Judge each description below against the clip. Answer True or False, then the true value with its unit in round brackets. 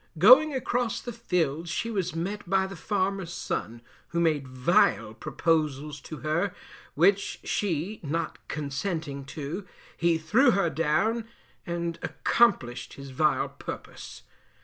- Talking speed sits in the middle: False (125 wpm)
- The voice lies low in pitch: False (170 Hz)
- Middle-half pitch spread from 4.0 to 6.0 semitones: True (4.9 semitones)